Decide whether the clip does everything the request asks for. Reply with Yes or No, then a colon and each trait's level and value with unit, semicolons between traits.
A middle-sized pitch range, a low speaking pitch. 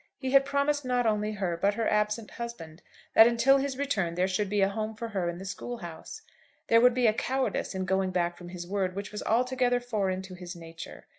No: average, 4.8 semitones; high, 210 Hz